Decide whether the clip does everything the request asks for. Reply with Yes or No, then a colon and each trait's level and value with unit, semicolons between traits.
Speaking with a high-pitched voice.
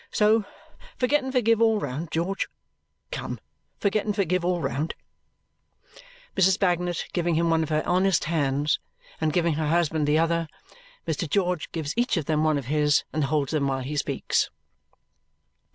No: medium, 165 Hz